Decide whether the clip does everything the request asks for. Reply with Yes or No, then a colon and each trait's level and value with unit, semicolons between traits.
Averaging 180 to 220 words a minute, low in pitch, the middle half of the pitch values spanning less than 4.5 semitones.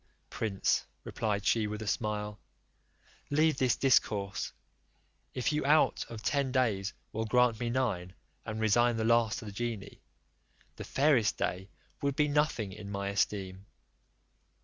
No: average, 145 wpm; low, 110 Hz; average, 3.9 semitones